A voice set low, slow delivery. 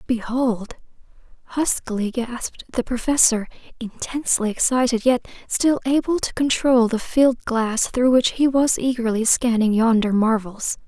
No: high, 240 Hz; slow, 125 wpm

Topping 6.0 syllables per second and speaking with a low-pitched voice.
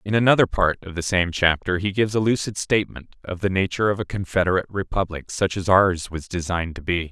Yes: 6.2 syllables/s; very low, 95 Hz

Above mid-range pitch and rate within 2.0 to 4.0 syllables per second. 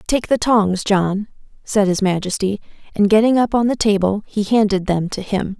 No: high, 205 Hz; 4.9 syllables/s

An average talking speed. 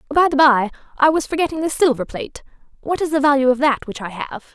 No: fast, 240 wpm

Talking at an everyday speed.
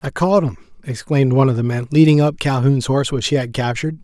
No: fast, 240 wpm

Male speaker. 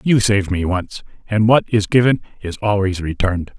Yes: male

